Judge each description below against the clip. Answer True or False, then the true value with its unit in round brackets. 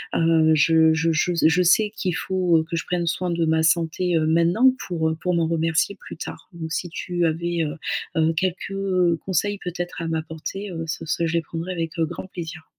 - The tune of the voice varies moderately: False (1.7 semitones)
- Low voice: False (165 Hz)